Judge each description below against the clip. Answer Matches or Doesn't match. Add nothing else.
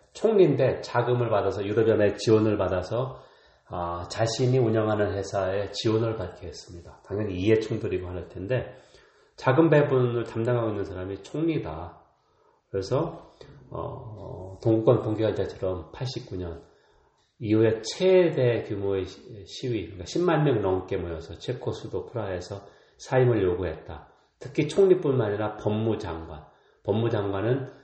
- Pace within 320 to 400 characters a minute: Doesn't match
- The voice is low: Matches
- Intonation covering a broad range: Doesn't match